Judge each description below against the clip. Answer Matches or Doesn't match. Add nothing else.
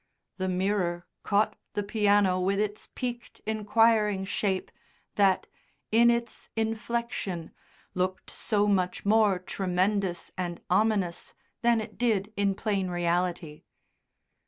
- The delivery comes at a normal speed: Doesn't match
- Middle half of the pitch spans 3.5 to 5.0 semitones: Doesn't match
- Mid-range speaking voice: Doesn't match